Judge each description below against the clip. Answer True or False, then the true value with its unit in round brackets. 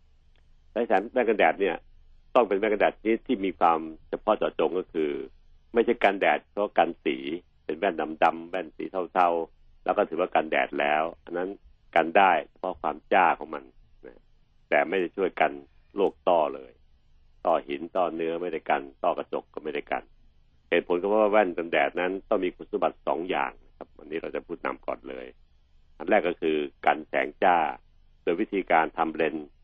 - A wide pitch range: False (3.8 semitones)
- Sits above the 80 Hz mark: False (75 Hz)